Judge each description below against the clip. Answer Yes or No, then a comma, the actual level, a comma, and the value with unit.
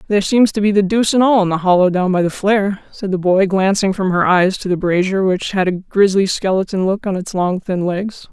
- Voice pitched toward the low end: No, high, 190 Hz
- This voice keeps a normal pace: No, fast, 260 wpm